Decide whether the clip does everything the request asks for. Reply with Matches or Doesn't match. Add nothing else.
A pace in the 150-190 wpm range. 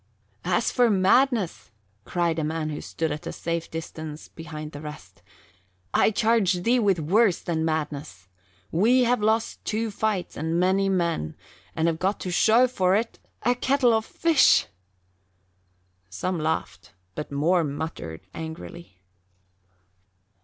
Doesn't match